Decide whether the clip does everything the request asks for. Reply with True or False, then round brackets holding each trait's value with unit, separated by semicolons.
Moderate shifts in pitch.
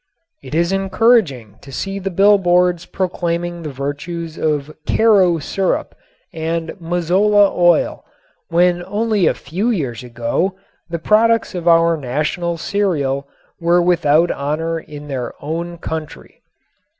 True (3.6 semitones)